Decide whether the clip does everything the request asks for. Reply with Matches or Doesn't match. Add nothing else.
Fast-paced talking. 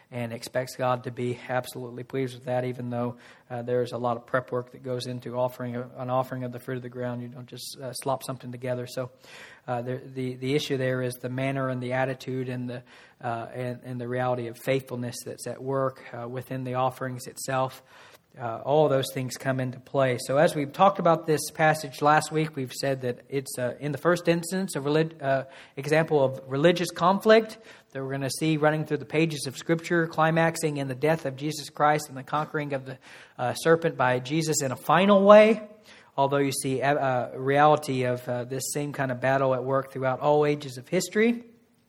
Matches